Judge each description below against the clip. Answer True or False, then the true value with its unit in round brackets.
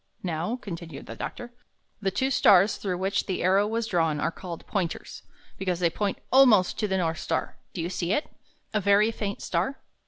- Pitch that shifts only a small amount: False (3.5 semitones)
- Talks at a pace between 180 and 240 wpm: True (190 wpm)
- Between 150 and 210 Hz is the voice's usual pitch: True (190 Hz)